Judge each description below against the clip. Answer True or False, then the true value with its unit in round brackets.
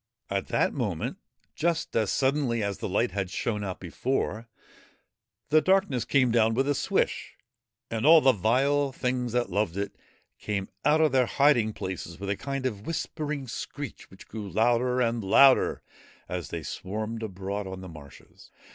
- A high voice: False (115 Hz)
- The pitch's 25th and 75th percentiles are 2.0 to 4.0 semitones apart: False (5.3 semitones)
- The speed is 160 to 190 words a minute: True (165 wpm)